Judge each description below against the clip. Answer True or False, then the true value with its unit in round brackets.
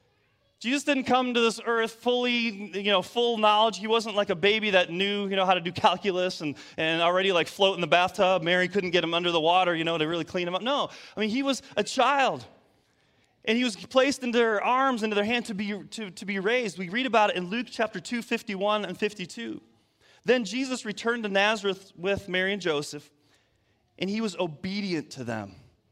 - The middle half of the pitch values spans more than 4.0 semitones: True (4.5 semitones)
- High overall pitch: True (200 Hz)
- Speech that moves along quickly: True (220 wpm)